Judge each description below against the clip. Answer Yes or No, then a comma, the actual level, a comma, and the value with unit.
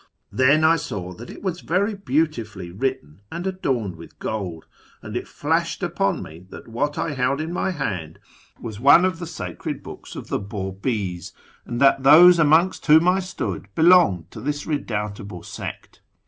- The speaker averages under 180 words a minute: Yes, average, 170 wpm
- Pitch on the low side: Yes, low, 130 Hz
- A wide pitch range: Yes, wide, 8.8 semitones